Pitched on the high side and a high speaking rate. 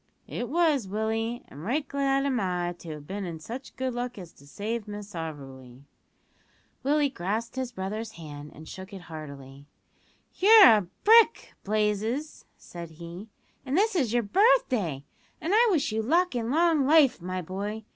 No: high, 220 Hz; average, 165 wpm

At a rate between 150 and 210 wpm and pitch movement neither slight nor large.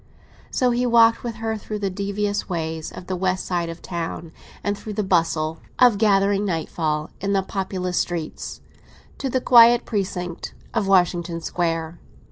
Yes: average, 160 wpm; average, 3.7 semitones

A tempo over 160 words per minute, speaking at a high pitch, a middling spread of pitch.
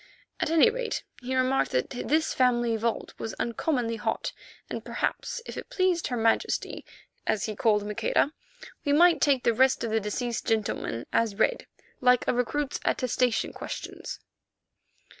No: average, 155 wpm; high, 245 Hz; average, 4.3 semitones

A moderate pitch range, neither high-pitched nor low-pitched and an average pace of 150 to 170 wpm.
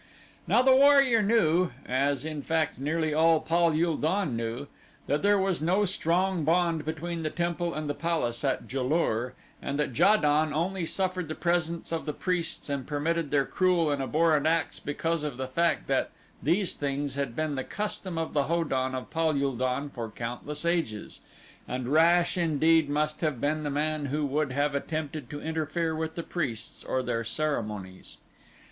No: average, 3.2 semitones; medium, 155 Hz; average, 185 wpm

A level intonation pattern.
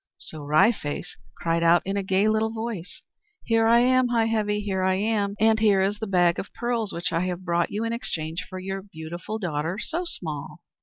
No: average, 4.3 semitones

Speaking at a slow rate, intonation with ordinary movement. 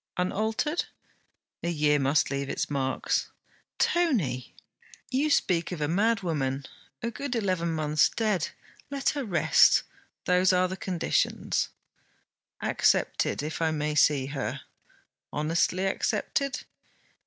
No: slow, 115 wpm; wide, 6.5 semitones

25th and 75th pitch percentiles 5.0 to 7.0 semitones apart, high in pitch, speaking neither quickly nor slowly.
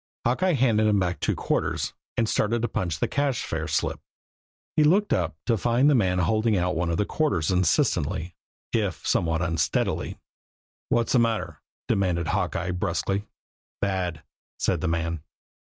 No: wide, 5.5 semitones; very low, 95 Hz; average, 155 wpm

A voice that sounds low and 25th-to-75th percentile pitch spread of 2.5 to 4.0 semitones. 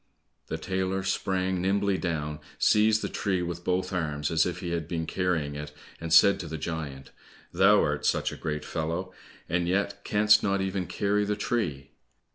Yes: very low, 90 Hz; average, 3.4 semitones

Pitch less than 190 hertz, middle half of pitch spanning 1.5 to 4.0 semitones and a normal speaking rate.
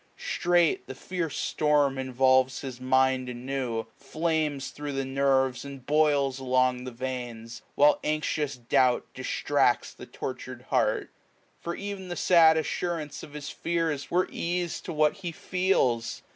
Yes: medium, 140 Hz; average, 3.6 semitones; average, 145 wpm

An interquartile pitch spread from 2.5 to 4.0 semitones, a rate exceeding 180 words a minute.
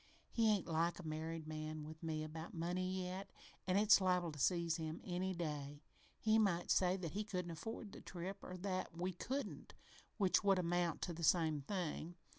Yes: average, 2.8 semitones; average, 190 wpm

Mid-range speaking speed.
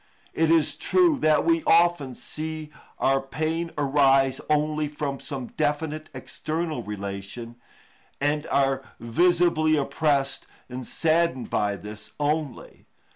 No: slow, 115 wpm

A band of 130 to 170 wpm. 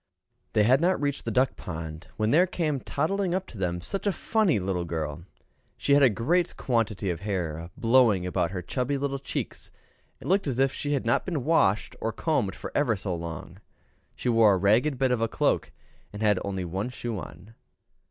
No: average, 200 wpm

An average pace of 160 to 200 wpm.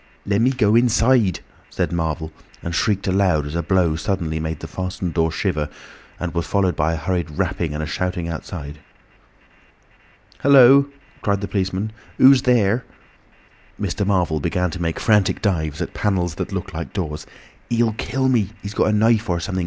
Yes: average, 170 wpm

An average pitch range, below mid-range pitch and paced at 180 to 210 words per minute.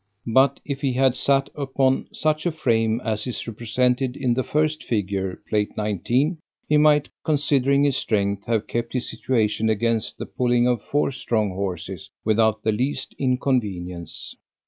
No: average, 4.3 semitones; low, 120 Hz; average, 155 wpm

